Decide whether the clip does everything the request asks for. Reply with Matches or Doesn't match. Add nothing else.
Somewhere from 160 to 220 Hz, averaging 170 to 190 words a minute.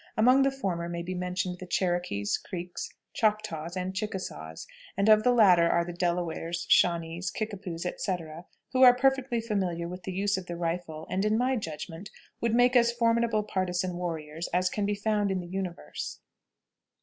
Matches